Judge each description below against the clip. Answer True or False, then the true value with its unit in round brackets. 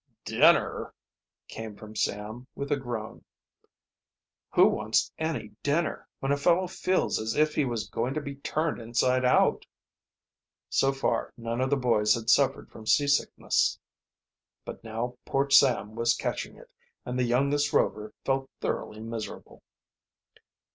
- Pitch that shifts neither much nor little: True (3.7 semitones)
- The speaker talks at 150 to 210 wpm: False (140 wpm)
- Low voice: True (125 Hz)